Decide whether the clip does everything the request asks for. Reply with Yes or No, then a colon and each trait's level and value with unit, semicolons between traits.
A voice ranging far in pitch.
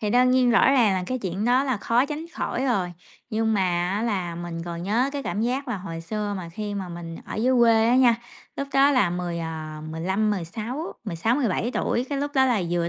Yes: wide, 6.1 semitones